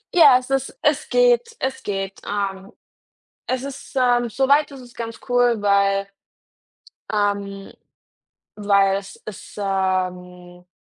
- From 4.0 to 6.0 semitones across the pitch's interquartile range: Yes, average, 4.8 semitones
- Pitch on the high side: Yes, high, 205 Hz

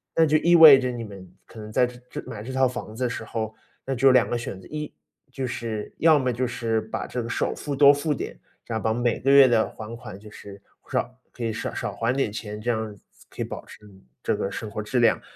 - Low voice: Yes, low, 120 Hz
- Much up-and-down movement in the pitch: No, average, 3.3 semitones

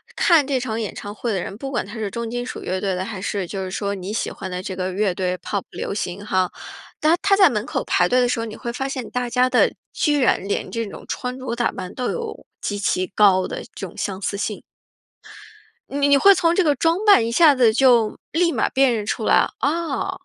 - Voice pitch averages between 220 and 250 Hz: Yes, high, 230 Hz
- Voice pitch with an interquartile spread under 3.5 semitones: No, average, 5.3 semitones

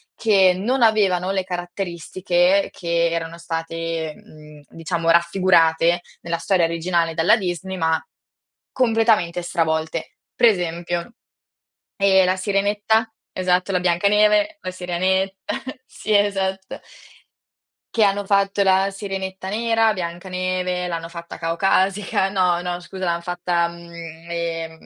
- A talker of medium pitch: Yes, medium, 180 Hz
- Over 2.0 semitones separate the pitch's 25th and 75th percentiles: Yes, narrow, 2.5 semitones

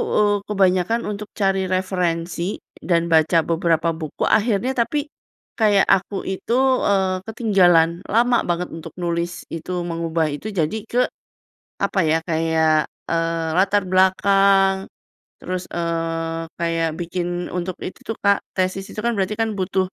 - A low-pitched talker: No, medium, 180 Hz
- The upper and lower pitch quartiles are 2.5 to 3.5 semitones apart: Yes, average, 3.1 semitones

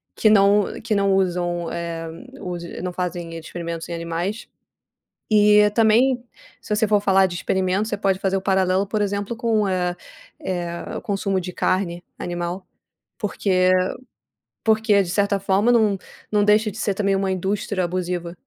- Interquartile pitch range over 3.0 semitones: No, average, 2.7 semitones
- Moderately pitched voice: No, high, 195 Hz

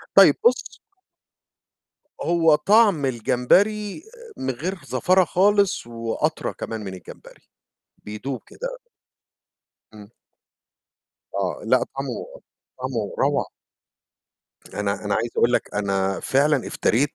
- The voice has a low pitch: Yes, low, 130 Hz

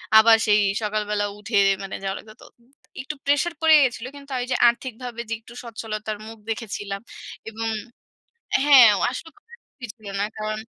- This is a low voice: No, high, 225 Hz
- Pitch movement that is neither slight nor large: Yes, average, 3.2 semitones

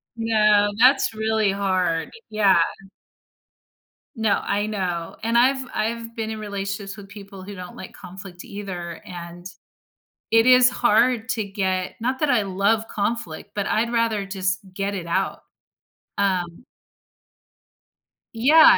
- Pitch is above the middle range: Yes, high, 205 Hz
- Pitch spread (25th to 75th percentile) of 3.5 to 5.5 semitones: No, average, 3.1 semitones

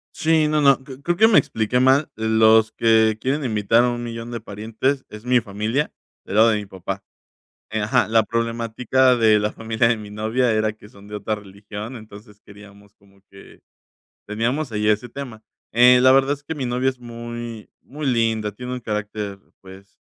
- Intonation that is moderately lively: Yes, average, 3.0 semitones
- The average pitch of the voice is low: Yes, low, 115 Hz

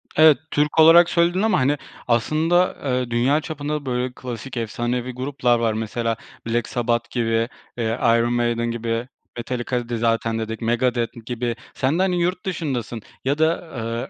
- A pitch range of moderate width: Yes, average, 4.0 semitones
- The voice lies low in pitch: Yes, low, 120 Hz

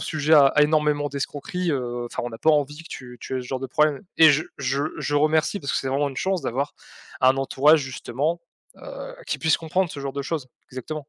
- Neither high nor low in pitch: Yes, medium, 145 Hz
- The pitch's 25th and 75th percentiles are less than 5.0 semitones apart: Yes, average, 2.8 semitones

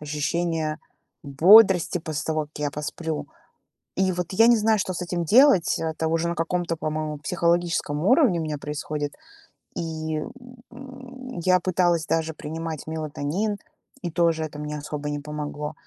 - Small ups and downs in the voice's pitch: No, average, 3.0 semitones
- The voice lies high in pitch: No, medium, 165 Hz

